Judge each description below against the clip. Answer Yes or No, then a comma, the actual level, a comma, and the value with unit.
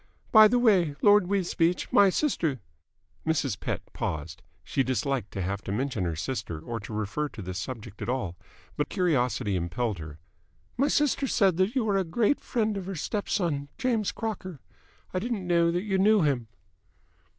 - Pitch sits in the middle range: Yes, medium, 160 Hz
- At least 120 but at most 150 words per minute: No, average, 185 wpm